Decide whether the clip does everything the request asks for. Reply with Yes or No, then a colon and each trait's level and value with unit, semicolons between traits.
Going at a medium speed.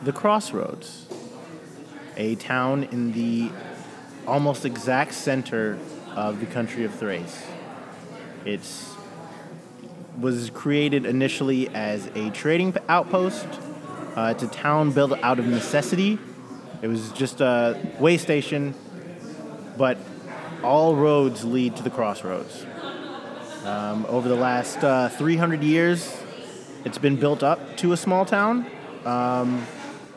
No: slow, 115 wpm